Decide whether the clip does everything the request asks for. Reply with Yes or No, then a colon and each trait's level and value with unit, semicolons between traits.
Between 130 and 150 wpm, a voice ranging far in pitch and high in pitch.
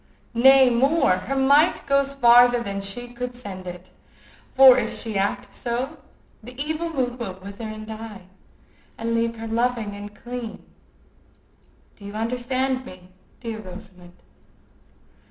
No: slow, 135 wpm; average, 3.7 semitones; high, 235 Hz